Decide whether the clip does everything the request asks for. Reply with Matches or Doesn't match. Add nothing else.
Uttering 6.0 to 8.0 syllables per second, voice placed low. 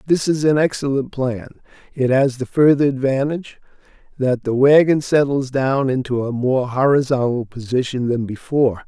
Doesn't match